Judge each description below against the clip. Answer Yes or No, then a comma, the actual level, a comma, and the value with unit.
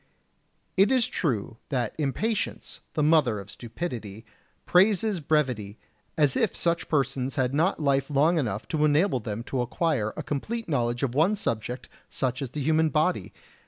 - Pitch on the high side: No, medium, 140 Hz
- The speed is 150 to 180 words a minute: Yes, average, 160 wpm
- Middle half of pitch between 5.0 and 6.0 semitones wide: Yes, average, 5.3 semitones